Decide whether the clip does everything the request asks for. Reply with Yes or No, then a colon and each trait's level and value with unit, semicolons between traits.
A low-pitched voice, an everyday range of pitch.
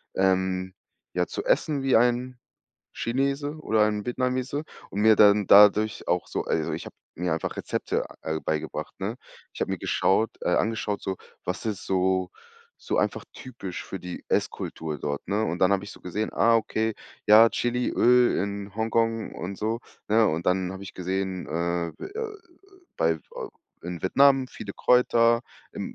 Yes: low, 105 Hz; average, 4.0 semitones